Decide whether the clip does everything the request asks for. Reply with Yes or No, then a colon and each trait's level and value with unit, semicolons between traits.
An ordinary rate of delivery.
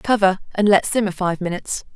Yes: average, 185 wpm